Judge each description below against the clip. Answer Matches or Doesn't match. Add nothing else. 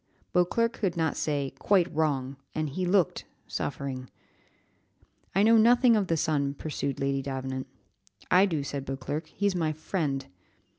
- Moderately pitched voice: Matches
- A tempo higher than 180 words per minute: Doesn't match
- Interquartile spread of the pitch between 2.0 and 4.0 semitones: Doesn't match